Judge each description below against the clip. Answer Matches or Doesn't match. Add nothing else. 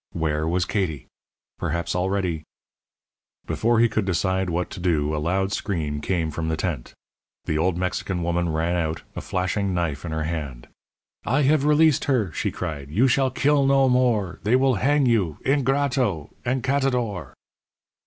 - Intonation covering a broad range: Matches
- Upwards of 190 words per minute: Doesn't match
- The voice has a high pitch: Doesn't match